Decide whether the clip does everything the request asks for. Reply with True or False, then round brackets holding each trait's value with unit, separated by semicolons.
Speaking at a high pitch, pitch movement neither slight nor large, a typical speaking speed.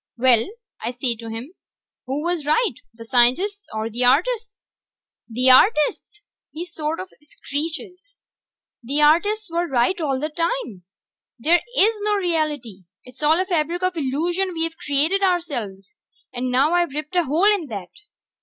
False (305 Hz; 5.8 semitones; 150 wpm)